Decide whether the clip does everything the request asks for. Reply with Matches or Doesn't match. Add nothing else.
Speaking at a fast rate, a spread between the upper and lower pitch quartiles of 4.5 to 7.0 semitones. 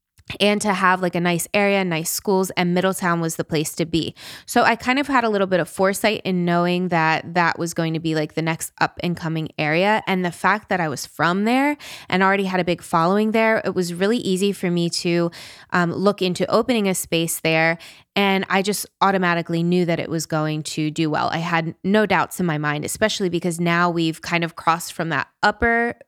Doesn't match